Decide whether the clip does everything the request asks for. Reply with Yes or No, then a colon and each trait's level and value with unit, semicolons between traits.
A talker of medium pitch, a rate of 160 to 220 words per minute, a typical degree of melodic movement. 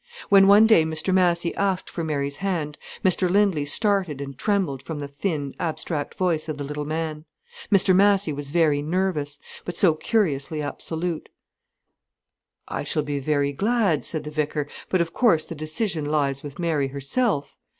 Yes: medium, 160 Hz; average, 165 wpm; average, 4.4 semitones